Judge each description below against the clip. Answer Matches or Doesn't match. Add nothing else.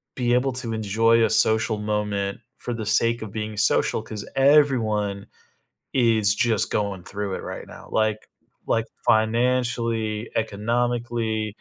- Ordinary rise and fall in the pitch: Doesn't match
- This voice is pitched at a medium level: Doesn't match